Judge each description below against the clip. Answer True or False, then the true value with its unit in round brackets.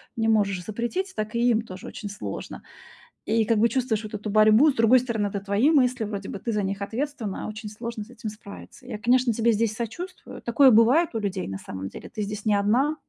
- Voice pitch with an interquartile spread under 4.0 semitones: True (2.9 semitones)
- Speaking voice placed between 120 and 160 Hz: False (220 Hz)